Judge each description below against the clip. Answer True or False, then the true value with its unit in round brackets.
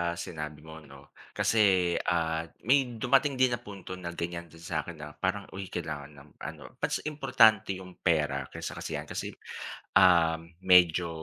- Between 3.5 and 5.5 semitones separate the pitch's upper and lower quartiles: True (4.4 semitones)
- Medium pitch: False (85 Hz)